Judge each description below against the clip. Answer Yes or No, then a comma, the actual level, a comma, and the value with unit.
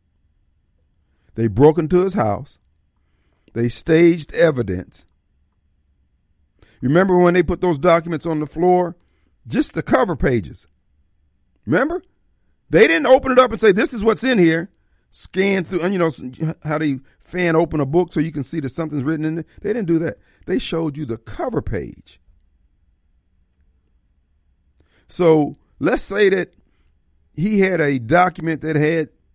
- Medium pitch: Yes, medium, 145 Hz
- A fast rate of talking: No, average, 150 wpm